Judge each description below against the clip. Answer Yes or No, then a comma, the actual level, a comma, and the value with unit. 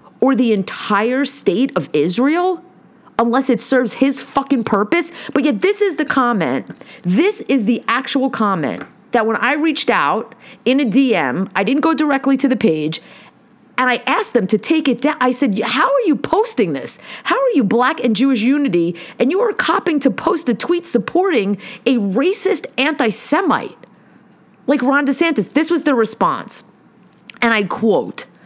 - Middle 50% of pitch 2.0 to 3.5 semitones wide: No, average, 4.7 semitones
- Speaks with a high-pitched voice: Yes, very high, 255 Hz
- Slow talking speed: No, average, 175 wpm